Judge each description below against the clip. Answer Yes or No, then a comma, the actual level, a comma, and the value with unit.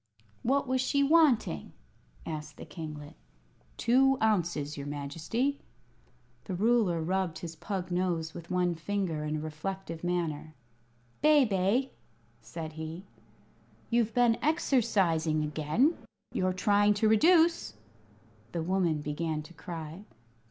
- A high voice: No, medium, 180 Hz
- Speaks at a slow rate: Yes, slow, 115 wpm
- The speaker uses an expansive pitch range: Yes, wide, 6.2 semitones